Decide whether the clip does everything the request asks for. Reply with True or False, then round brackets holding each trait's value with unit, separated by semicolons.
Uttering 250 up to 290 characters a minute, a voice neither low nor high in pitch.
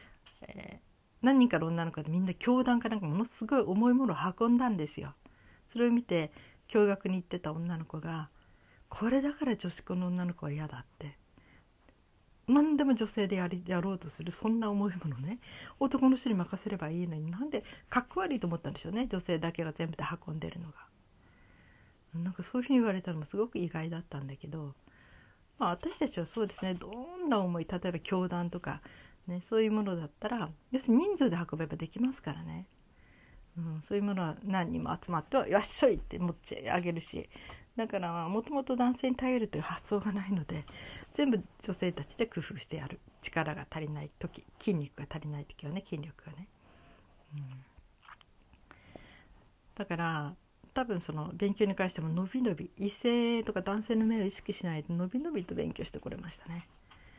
False (355 characters per minute; 180 Hz)